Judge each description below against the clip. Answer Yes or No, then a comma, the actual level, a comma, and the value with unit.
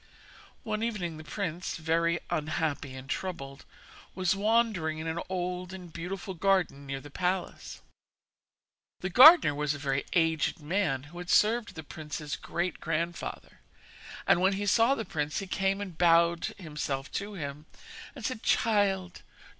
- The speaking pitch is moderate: Yes, medium, 175 Hz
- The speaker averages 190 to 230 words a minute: No, average, 150 wpm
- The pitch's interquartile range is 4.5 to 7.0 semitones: No, average, 4.1 semitones